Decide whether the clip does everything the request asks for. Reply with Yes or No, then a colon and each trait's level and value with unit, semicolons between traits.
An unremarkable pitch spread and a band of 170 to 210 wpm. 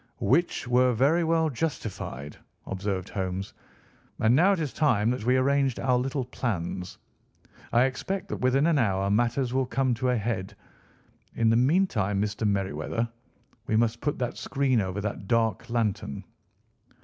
No: average, 4.6 semitones; average, 155 wpm